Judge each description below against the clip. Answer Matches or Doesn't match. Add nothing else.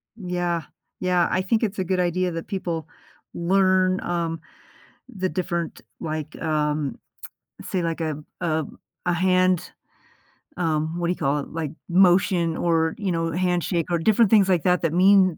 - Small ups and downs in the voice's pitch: Matches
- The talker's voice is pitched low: Doesn't match